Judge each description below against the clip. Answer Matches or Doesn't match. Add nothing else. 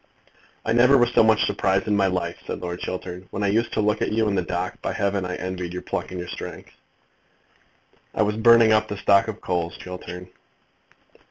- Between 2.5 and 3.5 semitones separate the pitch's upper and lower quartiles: Matches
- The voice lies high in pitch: Doesn't match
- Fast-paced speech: Matches